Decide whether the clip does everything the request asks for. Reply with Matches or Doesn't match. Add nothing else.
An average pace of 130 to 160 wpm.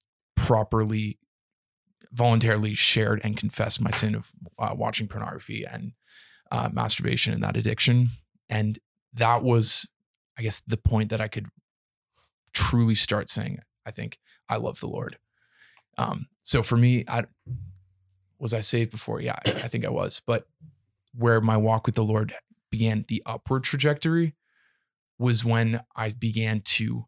Matches